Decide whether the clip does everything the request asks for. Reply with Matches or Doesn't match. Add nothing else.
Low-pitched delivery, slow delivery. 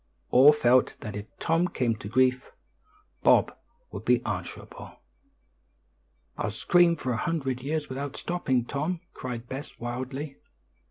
Matches